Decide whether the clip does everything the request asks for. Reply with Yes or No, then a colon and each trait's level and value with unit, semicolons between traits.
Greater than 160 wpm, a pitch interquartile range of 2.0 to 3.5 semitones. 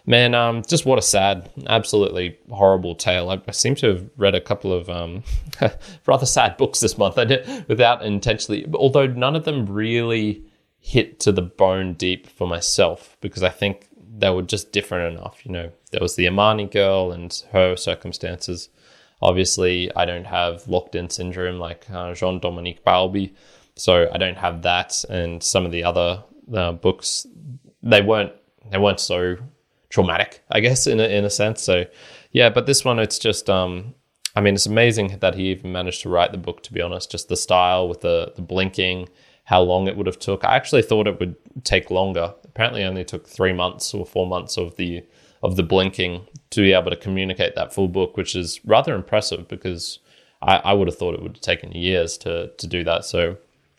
Yes: average, 200 wpm; average, 2.9 semitones